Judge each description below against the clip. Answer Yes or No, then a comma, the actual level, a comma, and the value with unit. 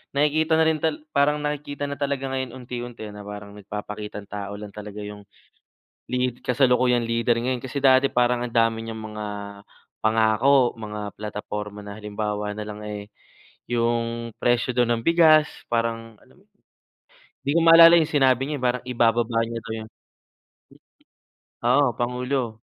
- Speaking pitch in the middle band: No, low, 120 Hz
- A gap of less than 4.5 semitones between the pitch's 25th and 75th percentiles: Yes, average, 3.9 semitones